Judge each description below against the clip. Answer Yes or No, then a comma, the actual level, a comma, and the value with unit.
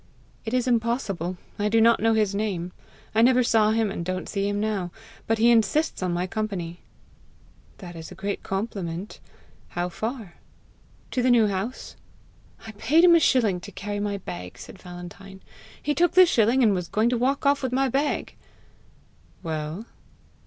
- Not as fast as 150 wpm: No, average, 175 wpm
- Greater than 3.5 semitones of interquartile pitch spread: Yes, average, 4.4 semitones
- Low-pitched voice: No, high, 215 Hz